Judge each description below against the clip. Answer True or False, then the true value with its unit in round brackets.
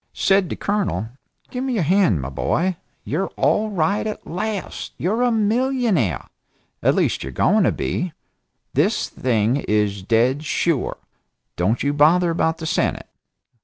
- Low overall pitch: False (170 Hz)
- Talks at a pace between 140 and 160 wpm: True (150 wpm)